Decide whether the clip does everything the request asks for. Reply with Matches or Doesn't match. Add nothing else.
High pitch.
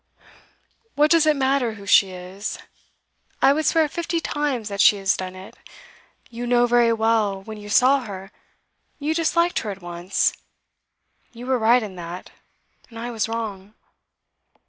Matches